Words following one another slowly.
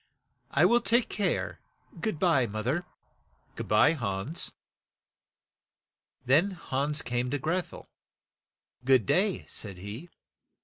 Yes: slow, 130 wpm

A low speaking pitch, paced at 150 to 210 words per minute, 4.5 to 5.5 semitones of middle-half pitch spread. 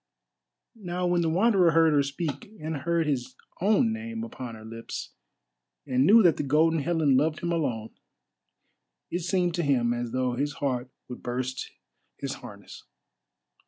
No: medium, 150 Hz; average, 160 wpm; average, 5.2 semitones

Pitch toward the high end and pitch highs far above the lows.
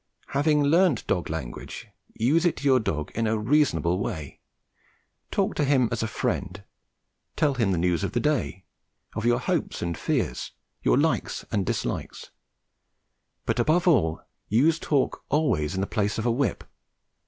No: low, 115 Hz; wide, 8.2 semitones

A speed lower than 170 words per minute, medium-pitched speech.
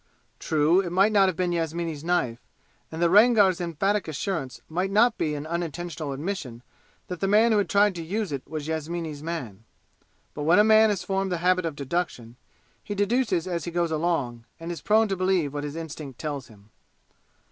No: average, 190 wpm; medium, 170 Hz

